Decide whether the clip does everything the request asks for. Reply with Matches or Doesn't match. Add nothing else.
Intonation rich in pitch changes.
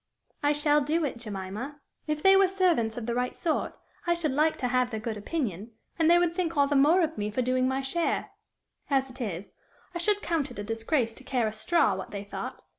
Matches